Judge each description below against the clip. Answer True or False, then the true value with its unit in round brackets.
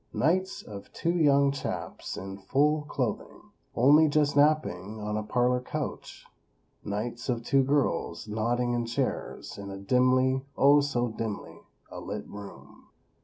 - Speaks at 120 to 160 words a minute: True (140 wpm)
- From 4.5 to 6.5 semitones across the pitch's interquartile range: True (5.0 semitones)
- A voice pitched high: False (125 Hz)